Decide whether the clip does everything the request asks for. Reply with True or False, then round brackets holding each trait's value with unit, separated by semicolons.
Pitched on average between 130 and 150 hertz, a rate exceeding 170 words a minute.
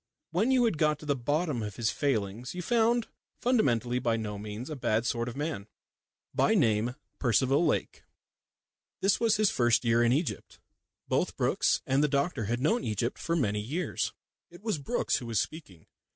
True (135 Hz; 180 wpm)